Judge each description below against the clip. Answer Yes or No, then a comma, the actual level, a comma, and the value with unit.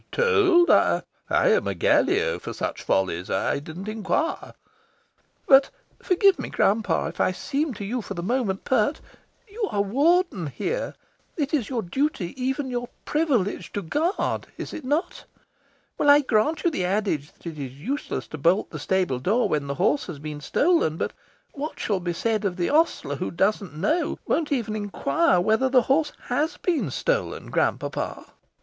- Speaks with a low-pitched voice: No, high, 225 Hz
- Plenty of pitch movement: Yes, wide, 9.0 semitones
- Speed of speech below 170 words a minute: No, average, 175 wpm